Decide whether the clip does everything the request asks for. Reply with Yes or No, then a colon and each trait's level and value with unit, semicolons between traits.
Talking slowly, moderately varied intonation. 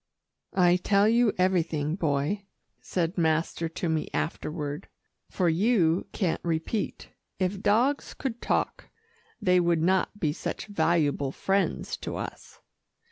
Yes: slow, 125 wpm; average, 3.8 semitones